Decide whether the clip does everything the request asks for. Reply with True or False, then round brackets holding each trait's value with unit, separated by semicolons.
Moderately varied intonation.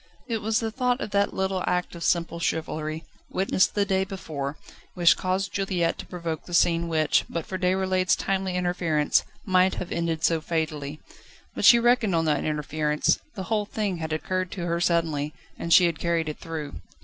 True (3.0 semitones)